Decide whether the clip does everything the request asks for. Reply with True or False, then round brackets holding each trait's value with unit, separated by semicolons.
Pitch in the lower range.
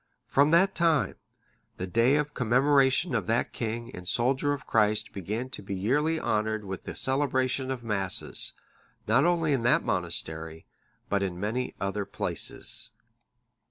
True (120 Hz)